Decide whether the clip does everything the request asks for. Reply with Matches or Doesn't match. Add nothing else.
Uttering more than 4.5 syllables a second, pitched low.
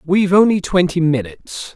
Doesn't match